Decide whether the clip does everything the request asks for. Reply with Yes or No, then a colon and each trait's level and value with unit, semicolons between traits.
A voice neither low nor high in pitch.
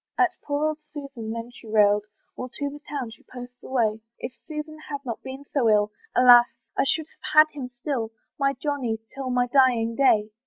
No: very high, 255 Hz